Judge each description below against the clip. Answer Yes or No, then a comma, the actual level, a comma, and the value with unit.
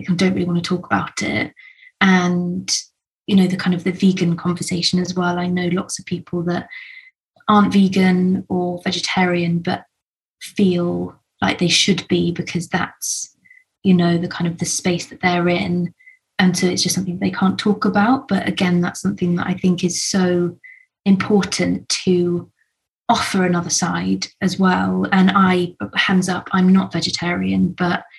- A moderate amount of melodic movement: No, narrow, 1.5 semitones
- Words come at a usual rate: Yes, average, 170 wpm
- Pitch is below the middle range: No, medium, 180 Hz